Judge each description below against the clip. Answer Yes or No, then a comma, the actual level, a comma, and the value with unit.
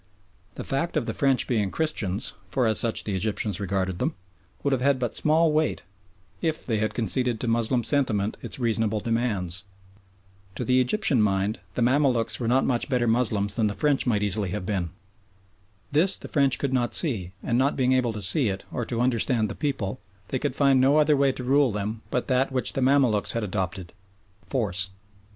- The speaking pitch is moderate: No, low, 120 Hz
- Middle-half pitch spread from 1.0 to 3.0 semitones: No, average, 4.4 semitones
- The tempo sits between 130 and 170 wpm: No, average, 195 wpm